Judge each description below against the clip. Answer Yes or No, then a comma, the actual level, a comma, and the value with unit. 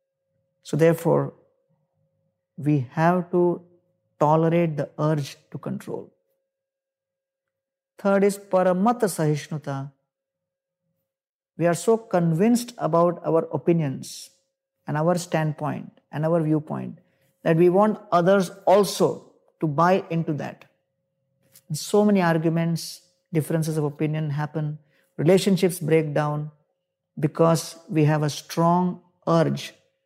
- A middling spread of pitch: Yes, average, 3.8 semitones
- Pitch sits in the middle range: Yes, medium, 170 Hz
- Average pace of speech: No, slow, 105 wpm